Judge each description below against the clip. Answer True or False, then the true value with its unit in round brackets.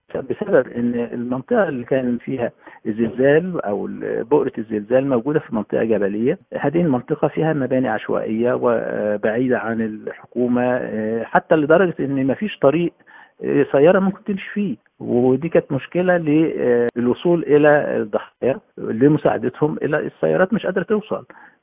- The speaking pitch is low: True (130 Hz)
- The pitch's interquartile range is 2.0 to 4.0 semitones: False (5.1 semitones)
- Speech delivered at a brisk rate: False (120 wpm)